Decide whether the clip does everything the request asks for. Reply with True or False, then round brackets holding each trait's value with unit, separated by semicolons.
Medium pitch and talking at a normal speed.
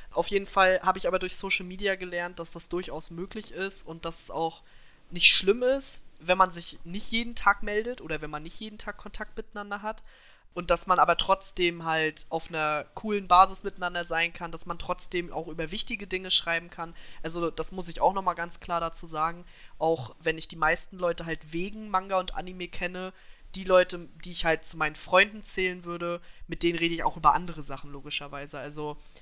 False (175 Hz; 210 wpm)